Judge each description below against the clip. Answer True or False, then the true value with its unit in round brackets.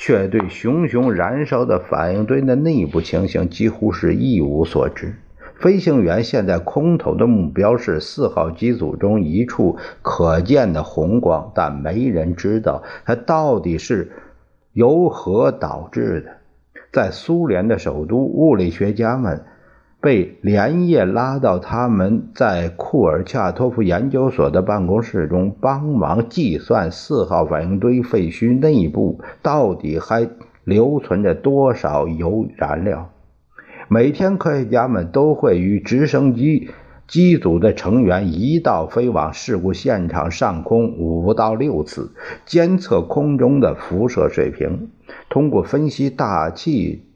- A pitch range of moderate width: False (6.9 semitones)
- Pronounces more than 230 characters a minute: False (205 characters per minute)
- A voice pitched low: True (115 Hz)